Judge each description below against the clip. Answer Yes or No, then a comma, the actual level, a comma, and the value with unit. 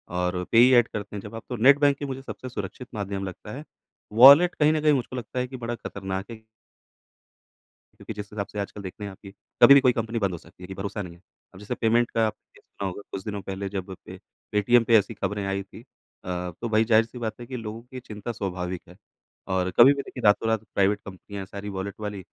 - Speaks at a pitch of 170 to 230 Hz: No, low, 105 Hz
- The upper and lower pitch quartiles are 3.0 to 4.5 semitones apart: Yes, average, 3.5 semitones